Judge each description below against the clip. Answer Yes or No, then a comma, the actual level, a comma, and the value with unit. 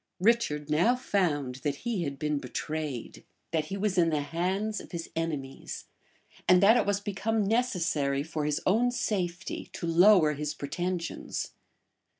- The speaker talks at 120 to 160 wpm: Yes, average, 155 wpm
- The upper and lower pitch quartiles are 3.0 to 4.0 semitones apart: No, average, 5.2 semitones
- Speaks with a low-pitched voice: No, medium, 170 Hz